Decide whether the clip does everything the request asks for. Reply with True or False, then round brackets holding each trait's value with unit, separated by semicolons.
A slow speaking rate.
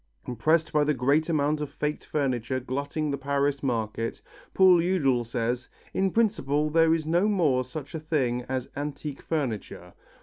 False (160 wpm)